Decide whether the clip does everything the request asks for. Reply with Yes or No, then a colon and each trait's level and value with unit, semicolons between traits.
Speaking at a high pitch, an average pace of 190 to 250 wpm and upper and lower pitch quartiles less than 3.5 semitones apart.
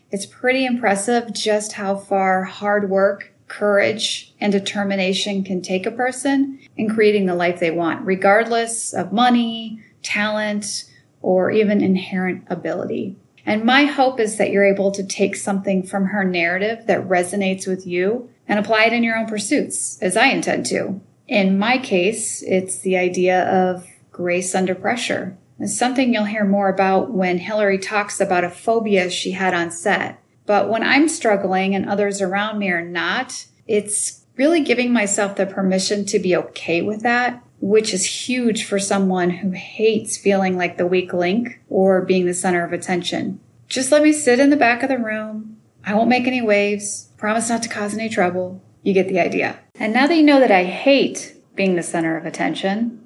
No: high, 200 Hz; average, 180 wpm; average, 3.1 semitones